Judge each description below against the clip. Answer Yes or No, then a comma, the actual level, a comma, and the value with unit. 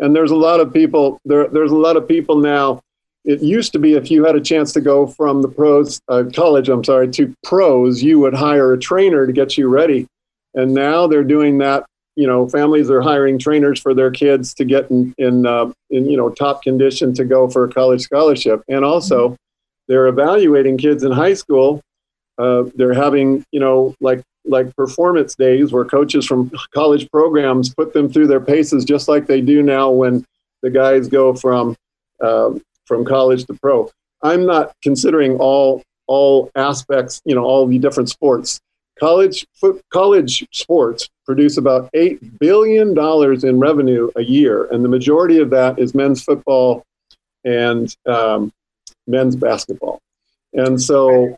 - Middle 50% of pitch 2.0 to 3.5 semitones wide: Yes, narrow, 2.5 semitones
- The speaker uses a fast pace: No, average, 180 wpm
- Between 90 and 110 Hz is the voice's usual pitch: No, low, 135 Hz